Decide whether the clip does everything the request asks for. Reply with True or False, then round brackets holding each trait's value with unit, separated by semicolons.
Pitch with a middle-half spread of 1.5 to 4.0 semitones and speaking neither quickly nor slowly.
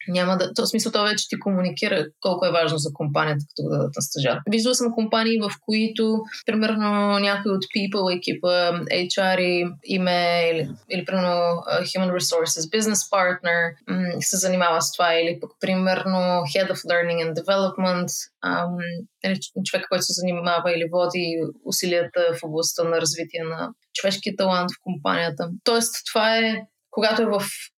True (2.8 semitones; 155 wpm)